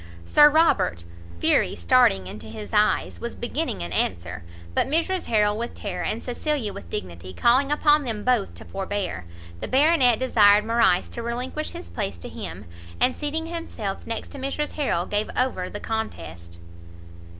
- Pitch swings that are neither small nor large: No, wide, 8.1 semitones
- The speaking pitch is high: Yes, high, 220 Hz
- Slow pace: No, average, 160 wpm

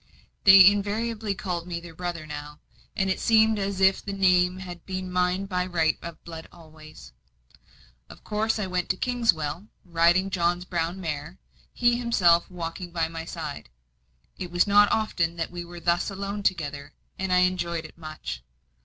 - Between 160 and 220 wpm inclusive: Yes, average, 170 wpm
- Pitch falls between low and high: Yes, medium, 180 Hz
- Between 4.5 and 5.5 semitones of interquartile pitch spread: No, average, 2.8 semitones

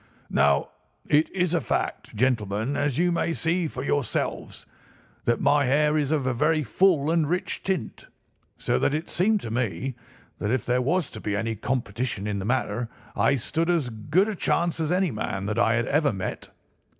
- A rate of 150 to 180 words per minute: No, average, 190 wpm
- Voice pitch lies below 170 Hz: Yes, medium, 140 Hz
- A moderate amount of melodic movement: No, wide, 6.3 semitones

